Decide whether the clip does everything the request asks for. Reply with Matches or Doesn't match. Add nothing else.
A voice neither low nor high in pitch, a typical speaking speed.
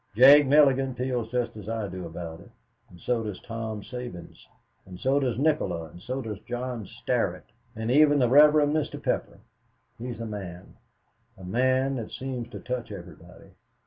Doesn't match